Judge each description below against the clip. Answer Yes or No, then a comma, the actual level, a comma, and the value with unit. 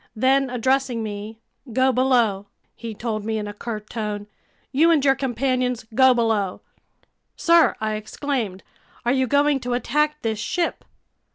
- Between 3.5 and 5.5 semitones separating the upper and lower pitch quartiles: Yes, average, 3.8 semitones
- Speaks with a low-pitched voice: No, high, 245 Hz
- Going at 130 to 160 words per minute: Yes, average, 150 wpm